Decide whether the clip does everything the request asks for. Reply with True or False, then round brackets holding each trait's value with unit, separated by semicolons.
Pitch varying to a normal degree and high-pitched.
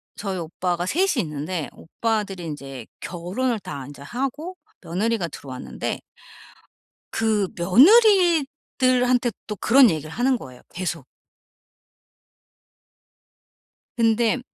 False (7.2 semitones; 210 Hz)